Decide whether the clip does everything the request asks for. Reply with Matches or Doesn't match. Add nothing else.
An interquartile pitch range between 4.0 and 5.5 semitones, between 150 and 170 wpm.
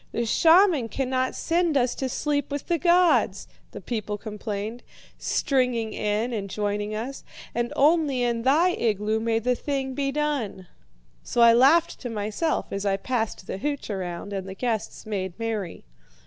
Matches